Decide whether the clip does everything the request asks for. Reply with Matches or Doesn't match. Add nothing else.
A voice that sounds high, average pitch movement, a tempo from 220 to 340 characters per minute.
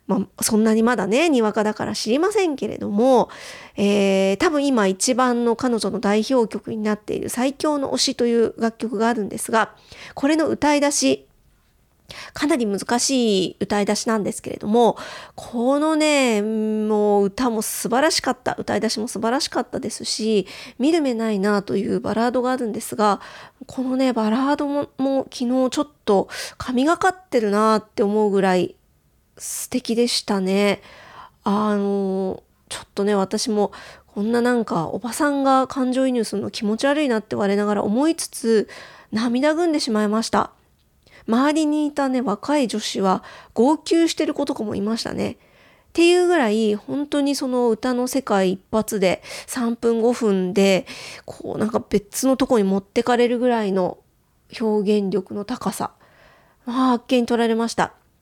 Matches